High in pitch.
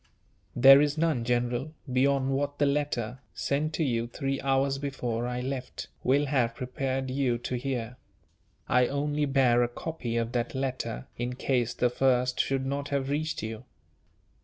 No: low, 130 Hz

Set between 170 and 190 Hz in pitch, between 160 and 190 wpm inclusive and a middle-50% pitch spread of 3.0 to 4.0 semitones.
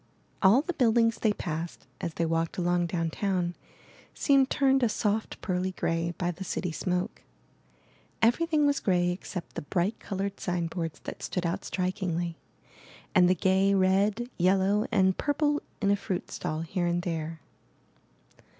No: medium, 185 Hz; average, 150 wpm; average, 3.4 semitones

